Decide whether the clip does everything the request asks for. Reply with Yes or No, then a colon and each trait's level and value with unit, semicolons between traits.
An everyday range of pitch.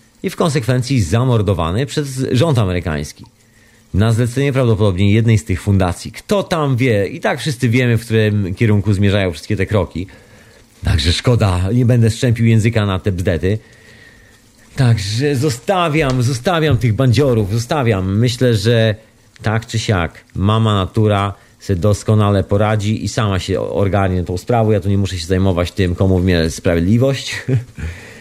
Yes: average, 3.5 semitones